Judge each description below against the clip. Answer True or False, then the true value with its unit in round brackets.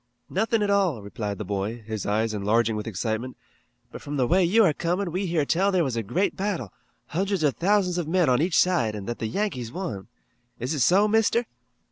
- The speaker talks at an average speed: False (215 wpm)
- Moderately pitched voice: True (150 Hz)